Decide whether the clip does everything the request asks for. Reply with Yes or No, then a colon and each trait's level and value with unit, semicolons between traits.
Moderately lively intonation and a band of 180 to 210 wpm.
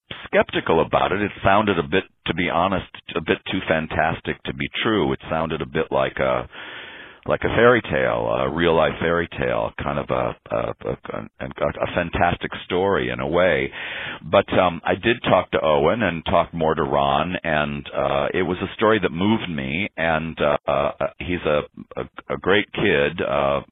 Yes: average, 3.2 semitones; average, 190 wpm